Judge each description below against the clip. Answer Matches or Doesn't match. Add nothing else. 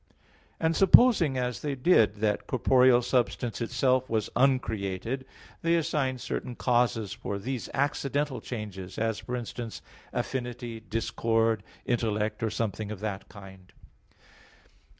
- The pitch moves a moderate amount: Matches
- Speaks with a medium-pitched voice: Doesn't match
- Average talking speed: Doesn't match